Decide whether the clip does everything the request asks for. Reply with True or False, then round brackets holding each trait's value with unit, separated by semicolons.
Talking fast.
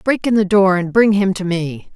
True (275 wpm)